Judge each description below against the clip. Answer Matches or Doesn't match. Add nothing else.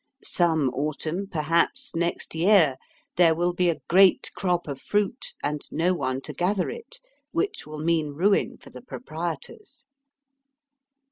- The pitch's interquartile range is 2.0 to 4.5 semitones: Matches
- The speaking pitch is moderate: Matches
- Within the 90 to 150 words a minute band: Matches